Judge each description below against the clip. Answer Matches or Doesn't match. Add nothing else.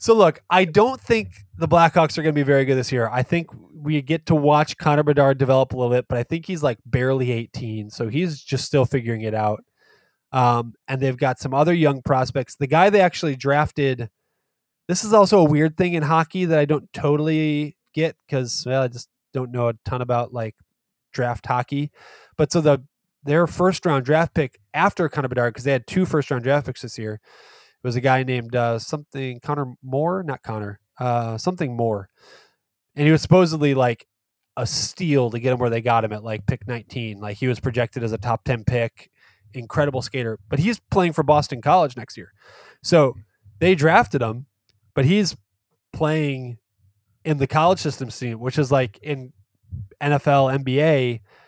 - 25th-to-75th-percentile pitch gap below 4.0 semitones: Doesn't match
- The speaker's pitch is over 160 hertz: Doesn't match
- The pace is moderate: Matches